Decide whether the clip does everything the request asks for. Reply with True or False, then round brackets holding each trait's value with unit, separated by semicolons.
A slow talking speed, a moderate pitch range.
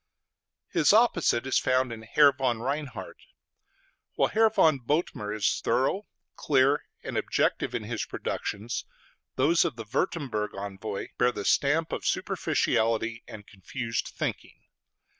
True (130 wpm; 4.9 semitones)